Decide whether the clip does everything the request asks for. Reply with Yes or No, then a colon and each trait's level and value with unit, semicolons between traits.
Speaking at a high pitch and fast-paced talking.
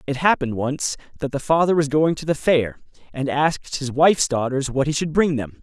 No: medium, 140 Hz; fast, 225 wpm